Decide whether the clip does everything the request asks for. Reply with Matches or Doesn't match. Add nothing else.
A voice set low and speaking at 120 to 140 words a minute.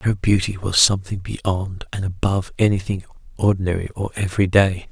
Matches